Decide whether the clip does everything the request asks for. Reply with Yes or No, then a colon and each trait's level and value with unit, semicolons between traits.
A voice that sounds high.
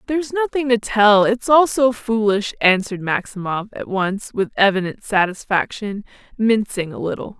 Yes: high, 215 Hz